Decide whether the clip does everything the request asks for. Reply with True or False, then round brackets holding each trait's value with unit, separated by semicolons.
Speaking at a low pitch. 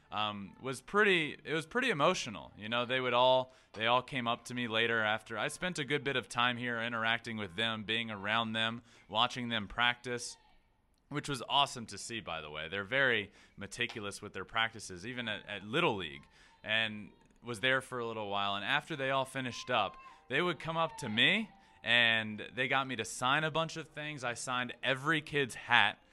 True (120 Hz)